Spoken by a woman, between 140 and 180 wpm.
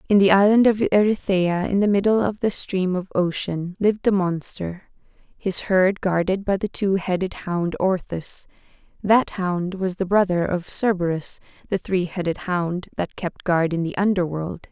Yes: female; average, 165 wpm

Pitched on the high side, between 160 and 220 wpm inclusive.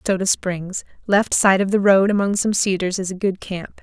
Yes: high, 195 Hz; fast, 205 wpm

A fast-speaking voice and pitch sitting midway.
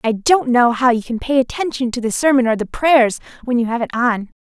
No: fast, 255 wpm; high, 245 Hz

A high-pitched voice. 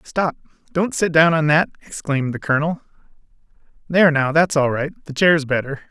No: medium, 150 Hz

